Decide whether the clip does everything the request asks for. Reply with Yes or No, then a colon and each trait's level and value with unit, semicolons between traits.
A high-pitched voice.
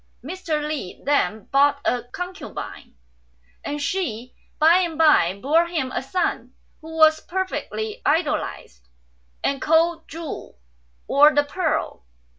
Yes: very high, 310 Hz